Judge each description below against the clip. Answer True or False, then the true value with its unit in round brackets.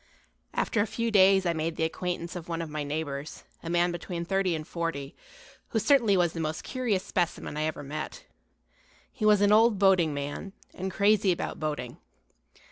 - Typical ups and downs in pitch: True (3.9 semitones)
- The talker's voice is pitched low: False (175 Hz)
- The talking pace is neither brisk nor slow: True (185 wpm)